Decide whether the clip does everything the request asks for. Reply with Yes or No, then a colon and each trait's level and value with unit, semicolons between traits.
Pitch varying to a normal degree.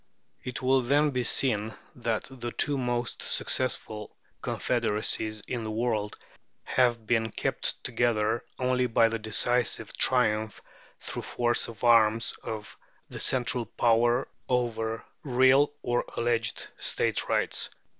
No: narrow, 2.1 semitones